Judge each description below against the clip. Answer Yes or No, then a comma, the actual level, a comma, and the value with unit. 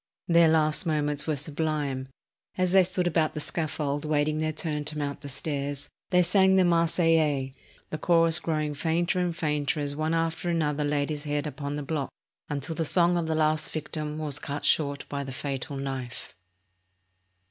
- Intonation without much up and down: Yes, narrow, 2.2 semitones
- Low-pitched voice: No, medium, 155 Hz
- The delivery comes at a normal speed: Yes, average, 180 wpm